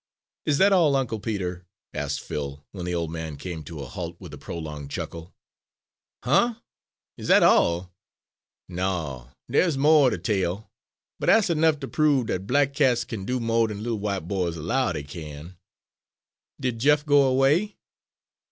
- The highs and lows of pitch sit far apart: Yes, wide, 8.3 semitones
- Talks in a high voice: No, low, 100 Hz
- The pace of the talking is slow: No, average, 170 wpm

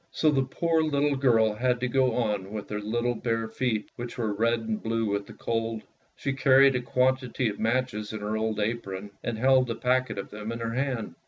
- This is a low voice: Yes, low, 115 Hz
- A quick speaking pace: Yes, fast, 220 wpm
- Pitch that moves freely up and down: No, average, 2.9 semitones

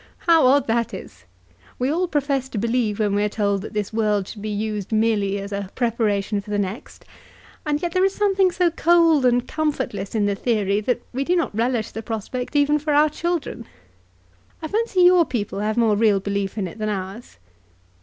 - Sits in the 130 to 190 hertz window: No, high, 230 Hz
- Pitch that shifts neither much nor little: No, wide, 6.3 semitones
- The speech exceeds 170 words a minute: Yes, average, 200 wpm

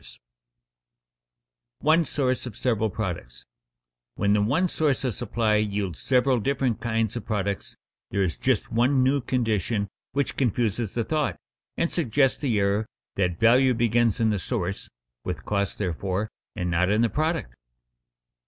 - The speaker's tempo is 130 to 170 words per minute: Yes, average, 150 wpm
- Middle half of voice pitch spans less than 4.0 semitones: No, average, 4.3 semitones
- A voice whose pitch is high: No, low, 110 Hz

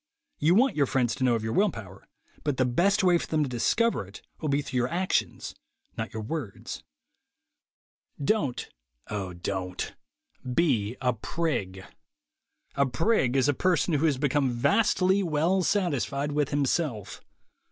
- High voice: No, medium, 140 Hz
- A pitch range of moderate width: No, wide, 6.0 semitones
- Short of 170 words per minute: Yes, average, 155 wpm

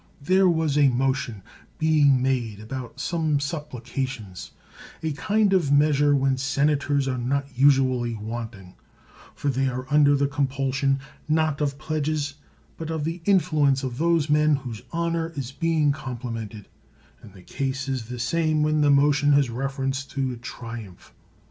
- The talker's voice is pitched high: No, medium, 140 Hz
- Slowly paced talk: No, average, 155 wpm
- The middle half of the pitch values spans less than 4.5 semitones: Yes, average, 2.9 semitones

